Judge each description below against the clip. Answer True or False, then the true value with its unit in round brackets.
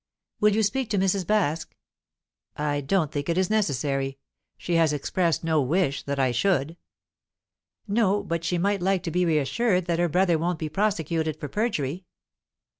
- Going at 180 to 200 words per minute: False (170 wpm)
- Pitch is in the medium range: True (170 Hz)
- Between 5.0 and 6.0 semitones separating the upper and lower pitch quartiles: False (4.5 semitones)